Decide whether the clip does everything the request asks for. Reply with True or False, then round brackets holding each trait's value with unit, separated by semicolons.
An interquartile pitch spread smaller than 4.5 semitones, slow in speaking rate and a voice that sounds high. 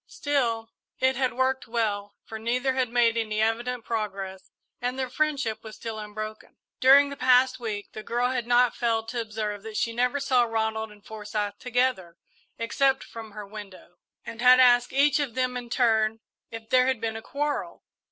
False (2.7 semitones; 180 wpm; 230 Hz)